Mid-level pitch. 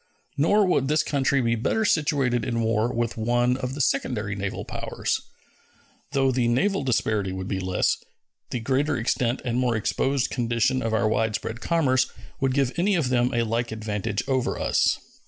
No: low, 120 Hz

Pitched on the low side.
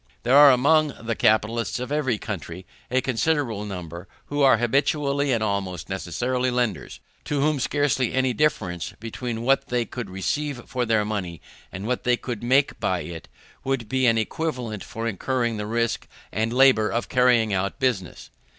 Yes: low, 120 Hz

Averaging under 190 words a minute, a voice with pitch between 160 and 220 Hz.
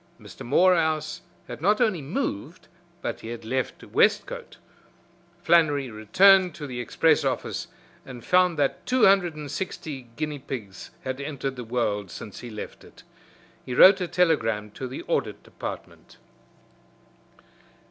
No: average, 140 wpm; medium, 140 Hz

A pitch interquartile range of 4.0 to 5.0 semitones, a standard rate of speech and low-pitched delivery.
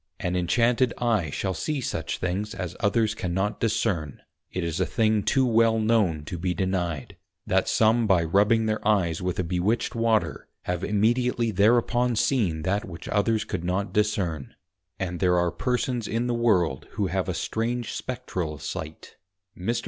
Yes: average, 4.4 semitones; average, 170 wpm; low, 100 Hz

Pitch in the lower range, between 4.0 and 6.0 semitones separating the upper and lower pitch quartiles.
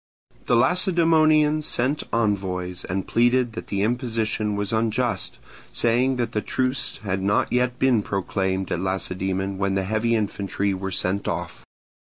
Yes: low, 110 Hz; average, 4.4 semitones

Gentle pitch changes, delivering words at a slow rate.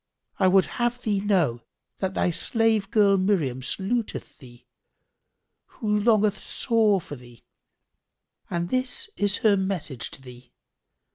No: average, 5.2 semitones; slow, 125 wpm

